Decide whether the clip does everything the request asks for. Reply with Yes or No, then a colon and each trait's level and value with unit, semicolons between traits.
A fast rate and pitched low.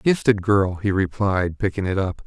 No: average, 185 wpm; low, 100 Hz